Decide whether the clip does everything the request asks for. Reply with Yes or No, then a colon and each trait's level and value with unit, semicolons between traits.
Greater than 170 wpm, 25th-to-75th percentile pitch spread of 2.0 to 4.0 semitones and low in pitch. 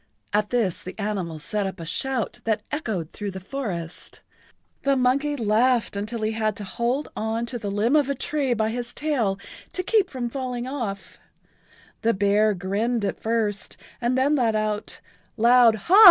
No: average, 180 wpm; average, 3.7 semitones; high, 225 Hz